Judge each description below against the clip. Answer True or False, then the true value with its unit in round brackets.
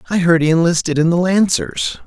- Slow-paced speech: False (205 wpm)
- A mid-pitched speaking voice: True (160 Hz)